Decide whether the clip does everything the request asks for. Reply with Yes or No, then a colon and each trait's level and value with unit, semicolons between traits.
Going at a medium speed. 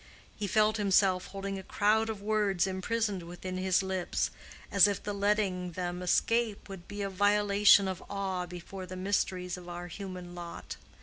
Yes: average, 170 wpm